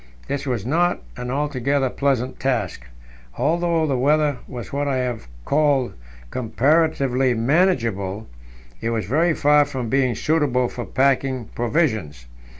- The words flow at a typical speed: No, slow, 130 wpm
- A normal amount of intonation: Yes, average, 3.6 semitones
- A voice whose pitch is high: No, low, 135 Hz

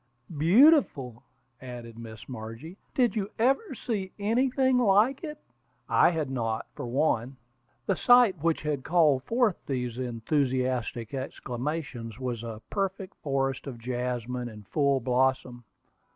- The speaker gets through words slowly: Yes, slow, 125 wpm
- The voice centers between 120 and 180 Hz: Yes, low, 135 Hz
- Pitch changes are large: Yes, wide, 8.0 semitones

